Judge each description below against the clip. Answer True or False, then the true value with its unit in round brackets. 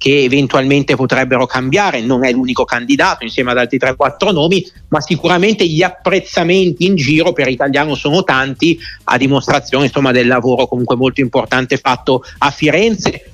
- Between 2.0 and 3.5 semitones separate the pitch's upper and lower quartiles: False (5.0 semitones)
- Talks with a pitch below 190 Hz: True (140 Hz)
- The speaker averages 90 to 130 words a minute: False (155 wpm)